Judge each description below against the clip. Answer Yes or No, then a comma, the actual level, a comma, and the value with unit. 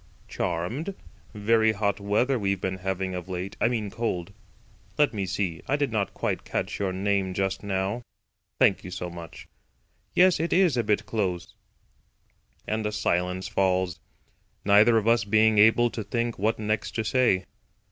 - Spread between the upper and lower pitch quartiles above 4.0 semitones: No, average, 3.4 semitones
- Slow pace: No, average, 160 wpm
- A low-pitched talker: Yes, low, 100 Hz